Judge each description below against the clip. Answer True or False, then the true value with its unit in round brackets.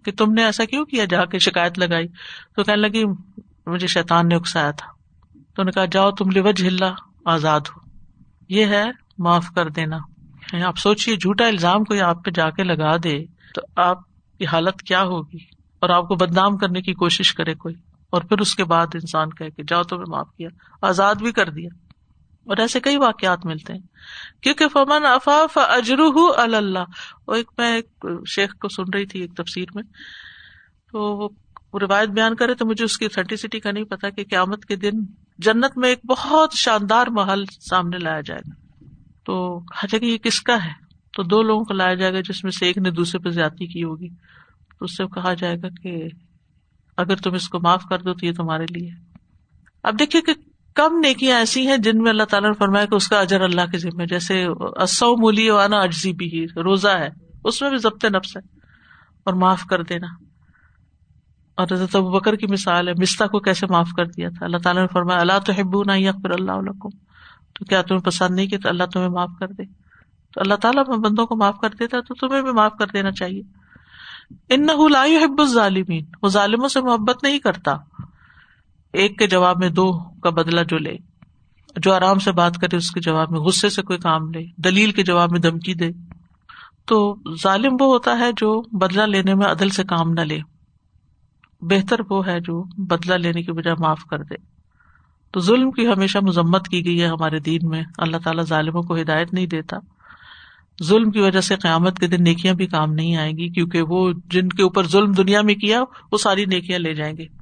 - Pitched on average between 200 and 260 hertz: False (190 Hz)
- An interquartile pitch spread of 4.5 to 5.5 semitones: False (3.5 semitones)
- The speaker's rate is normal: False (205 wpm)